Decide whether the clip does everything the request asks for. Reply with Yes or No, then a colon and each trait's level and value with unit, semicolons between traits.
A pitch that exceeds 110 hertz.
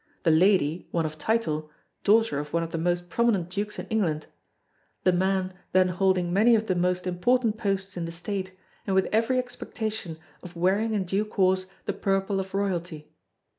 Yes: high, 190 Hz